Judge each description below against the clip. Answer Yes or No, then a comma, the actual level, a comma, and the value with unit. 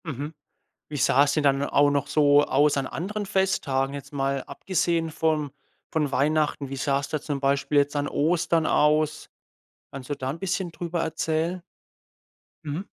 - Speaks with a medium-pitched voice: Yes, medium, 150 Hz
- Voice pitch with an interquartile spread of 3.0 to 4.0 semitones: No, narrow, 2.5 semitones